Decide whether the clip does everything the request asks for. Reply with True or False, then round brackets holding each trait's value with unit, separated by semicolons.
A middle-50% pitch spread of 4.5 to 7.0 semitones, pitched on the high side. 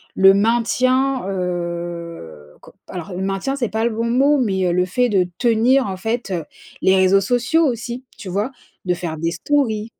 True (5.3 semitones; 200 Hz)